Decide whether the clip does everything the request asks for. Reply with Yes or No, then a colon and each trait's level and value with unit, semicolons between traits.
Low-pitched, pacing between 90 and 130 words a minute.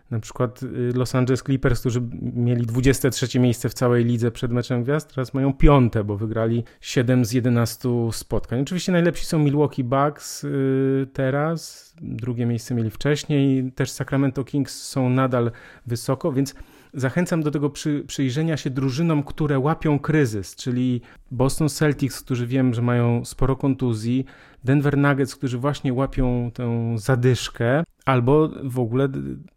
No: low, 130 Hz; average, 140 wpm